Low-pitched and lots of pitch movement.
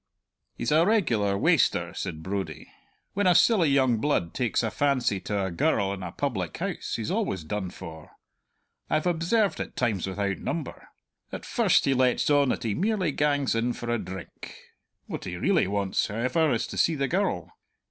Yes: low, 120 Hz; wide, 7.6 semitones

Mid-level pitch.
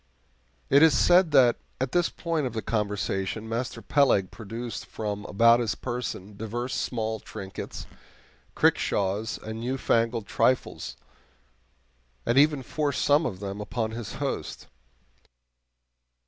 No: low, 115 Hz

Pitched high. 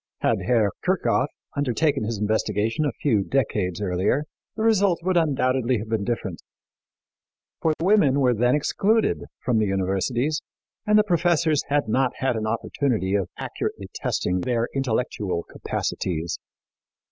No: low, 125 Hz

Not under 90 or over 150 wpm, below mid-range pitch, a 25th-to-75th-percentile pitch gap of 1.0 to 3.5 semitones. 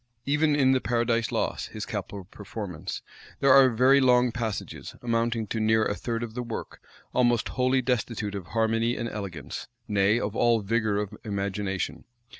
No: average, 165 wpm; low, 115 Hz; average, 3.0 semitones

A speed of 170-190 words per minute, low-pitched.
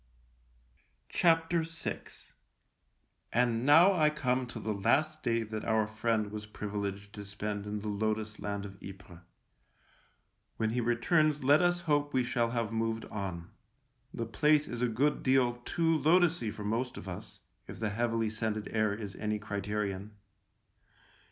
No: average, 150 wpm; low, 115 Hz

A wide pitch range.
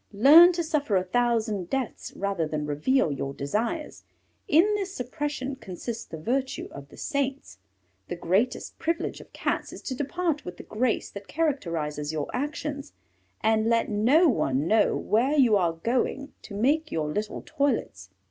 Yes: wide, 8.1 semitones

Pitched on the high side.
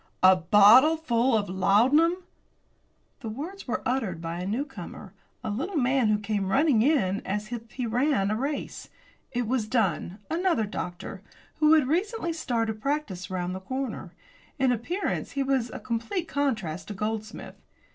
Yes: high, 235 Hz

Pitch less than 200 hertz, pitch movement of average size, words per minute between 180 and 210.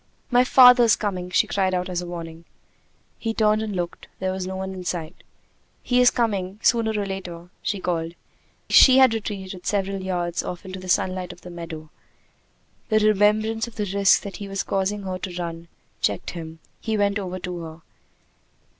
Yes: high, 190 Hz; average, 3.0 semitones; average, 185 wpm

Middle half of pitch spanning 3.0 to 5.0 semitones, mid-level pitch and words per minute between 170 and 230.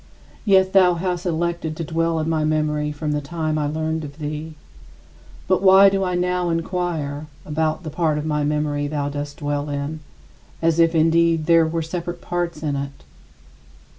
No: narrow, 2.4 semitones; medium, 160 Hz; average, 175 wpm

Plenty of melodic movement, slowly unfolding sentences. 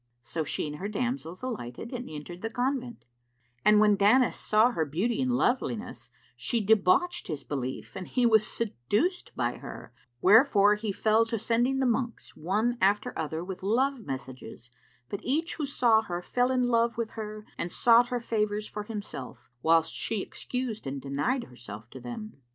No: wide, 6.1 semitones; average, 175 wpm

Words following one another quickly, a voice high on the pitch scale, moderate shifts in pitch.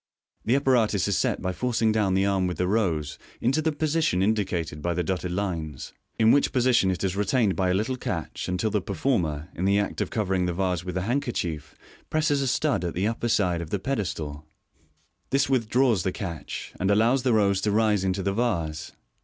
No: fast, 210 wpm; low, 100 Hz; average, 4.7 semitones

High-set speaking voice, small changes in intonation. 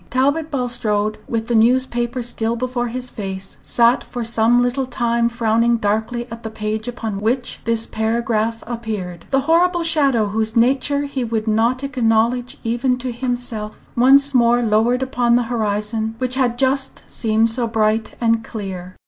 Yes: high, 235 Hz; narrow, 2.2 semitones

